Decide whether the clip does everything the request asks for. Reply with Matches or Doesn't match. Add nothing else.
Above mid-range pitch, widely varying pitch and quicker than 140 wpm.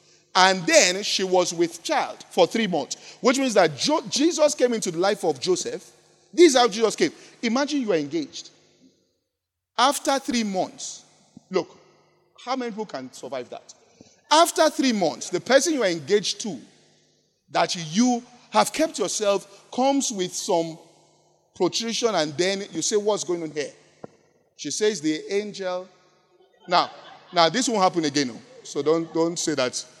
Matches